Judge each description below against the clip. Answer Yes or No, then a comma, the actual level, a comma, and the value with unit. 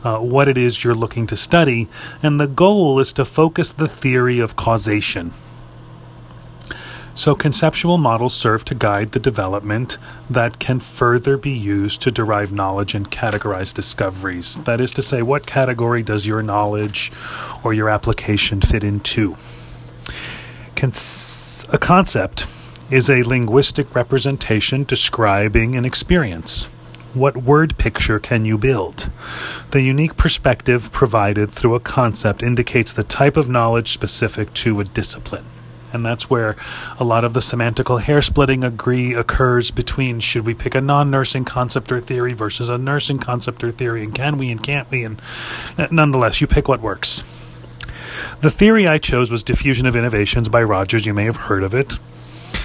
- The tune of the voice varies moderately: Yes, average, 3.5 semitones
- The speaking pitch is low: Yes, low, 120 Hz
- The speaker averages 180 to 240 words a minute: No, average, 155 wpm